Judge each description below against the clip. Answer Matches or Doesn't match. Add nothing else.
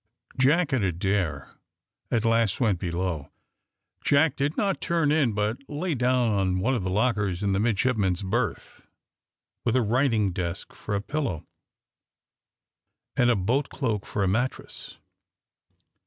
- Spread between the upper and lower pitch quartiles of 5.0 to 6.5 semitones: Matches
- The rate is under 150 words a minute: Matches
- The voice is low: Matches